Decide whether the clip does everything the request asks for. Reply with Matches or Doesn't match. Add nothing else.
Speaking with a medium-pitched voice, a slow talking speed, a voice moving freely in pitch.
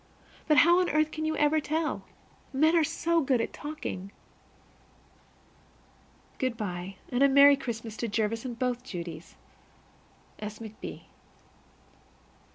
Doesn't match